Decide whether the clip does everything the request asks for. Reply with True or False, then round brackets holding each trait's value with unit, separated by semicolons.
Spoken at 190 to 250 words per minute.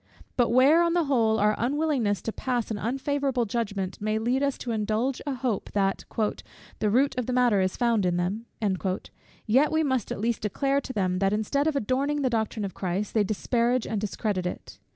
True (200 wpm)